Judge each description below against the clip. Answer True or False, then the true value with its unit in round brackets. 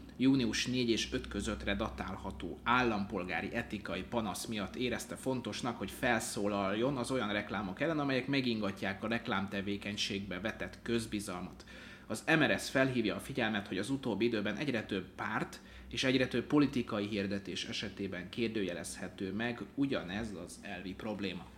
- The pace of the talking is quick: False (135 wpm)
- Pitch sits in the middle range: False (110 Hz)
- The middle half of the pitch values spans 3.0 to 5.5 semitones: True (3.6 semitones)